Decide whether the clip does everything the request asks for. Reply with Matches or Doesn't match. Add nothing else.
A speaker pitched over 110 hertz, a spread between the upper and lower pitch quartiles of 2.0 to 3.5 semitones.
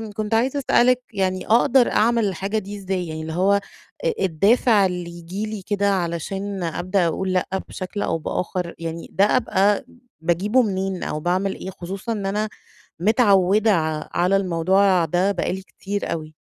Matches